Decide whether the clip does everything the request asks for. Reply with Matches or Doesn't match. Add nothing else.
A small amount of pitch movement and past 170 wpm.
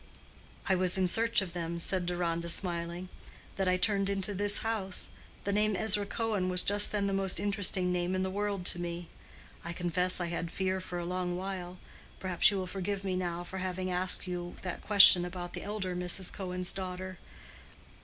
Matches